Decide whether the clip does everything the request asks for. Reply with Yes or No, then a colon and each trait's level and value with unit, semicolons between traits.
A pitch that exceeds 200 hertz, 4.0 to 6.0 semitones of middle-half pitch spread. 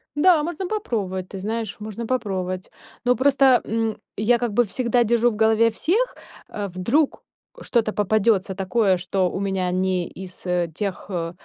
Yes: high, 215 Hz; average, 4.3 semitones